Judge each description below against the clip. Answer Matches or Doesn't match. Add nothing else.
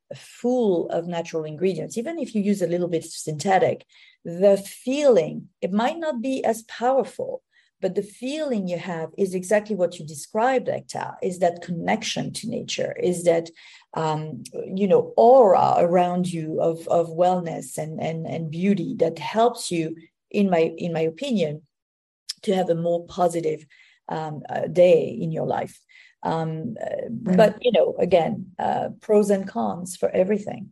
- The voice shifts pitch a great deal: Matches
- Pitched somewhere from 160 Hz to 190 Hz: Matches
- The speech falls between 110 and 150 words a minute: Doesn't match